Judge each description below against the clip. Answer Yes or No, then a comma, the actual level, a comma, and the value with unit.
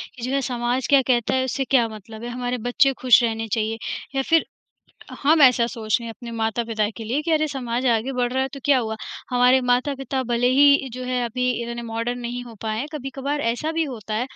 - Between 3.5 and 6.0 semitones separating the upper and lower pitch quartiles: No, narrow, 2.5 semitones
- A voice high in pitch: Yes, high, 245 Hz